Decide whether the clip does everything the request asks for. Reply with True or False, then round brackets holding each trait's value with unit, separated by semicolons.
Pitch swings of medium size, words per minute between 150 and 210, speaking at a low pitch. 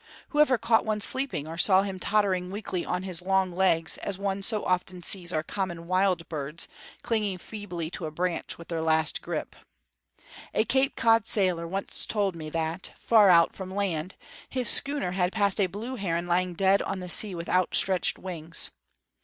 False (3.0 semitones; 185 wpm; 185 Hz)